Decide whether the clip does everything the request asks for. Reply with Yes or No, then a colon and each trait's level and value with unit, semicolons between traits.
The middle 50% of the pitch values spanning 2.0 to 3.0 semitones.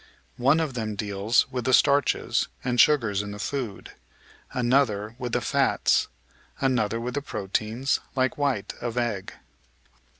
No: average, 3.9 semitones